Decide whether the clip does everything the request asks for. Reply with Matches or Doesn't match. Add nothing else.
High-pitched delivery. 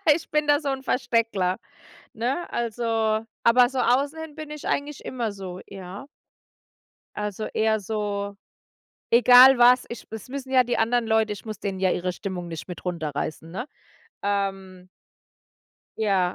Matches